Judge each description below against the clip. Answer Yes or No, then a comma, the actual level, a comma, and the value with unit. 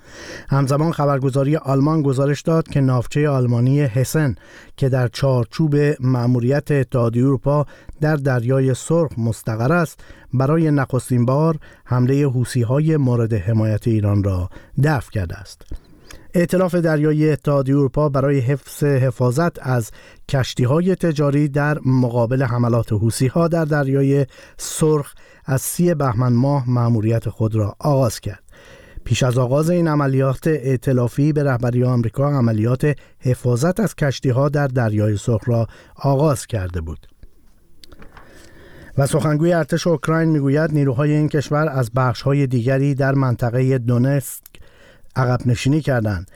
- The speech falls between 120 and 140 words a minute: Yes, average, 125 wpm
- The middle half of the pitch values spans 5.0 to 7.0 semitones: No, average, 3.4 semitones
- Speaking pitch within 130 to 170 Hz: Yes, low, 135 Hz